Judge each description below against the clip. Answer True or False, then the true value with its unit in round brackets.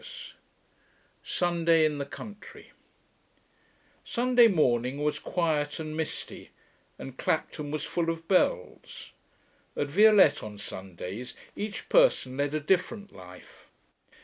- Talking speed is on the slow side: True (120 wpm)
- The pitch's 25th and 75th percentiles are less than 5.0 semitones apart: False (5.3 semitones)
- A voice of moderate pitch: True (155 Hz)